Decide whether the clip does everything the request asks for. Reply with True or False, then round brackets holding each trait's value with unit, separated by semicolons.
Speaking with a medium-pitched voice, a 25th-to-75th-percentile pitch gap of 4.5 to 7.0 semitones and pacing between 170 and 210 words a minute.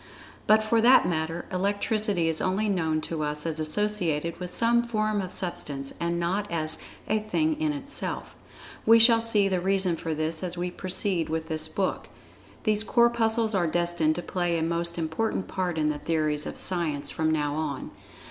True (175 Hz; 4.9 semitones; 180 wpm)